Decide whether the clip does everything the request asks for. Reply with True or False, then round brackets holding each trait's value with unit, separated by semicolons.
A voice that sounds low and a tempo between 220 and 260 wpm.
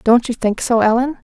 False (240 Hz; 225 wpm)